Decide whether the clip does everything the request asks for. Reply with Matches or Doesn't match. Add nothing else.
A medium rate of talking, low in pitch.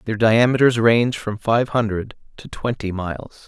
Matches